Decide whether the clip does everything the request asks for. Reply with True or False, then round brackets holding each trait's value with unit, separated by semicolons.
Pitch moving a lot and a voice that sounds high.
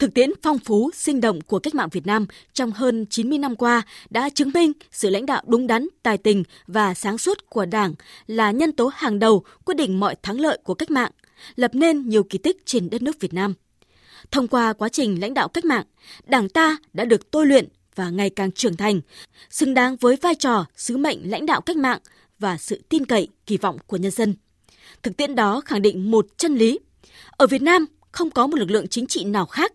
True (5.9 semitones; 235 Hz)